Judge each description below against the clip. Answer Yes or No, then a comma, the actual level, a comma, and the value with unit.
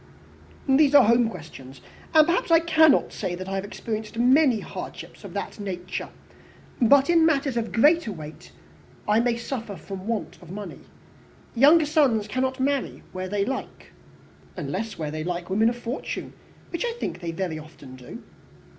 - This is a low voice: No, high, 225 Hz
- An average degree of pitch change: No, wide, 6.9 semitones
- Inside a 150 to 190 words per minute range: Yes, average, 170 wpm